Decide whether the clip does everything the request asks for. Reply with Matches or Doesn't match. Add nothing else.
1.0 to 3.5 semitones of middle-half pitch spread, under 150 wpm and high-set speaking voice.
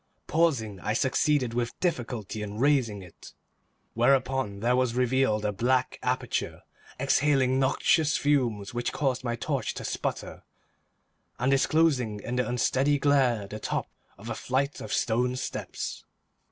Doesn't match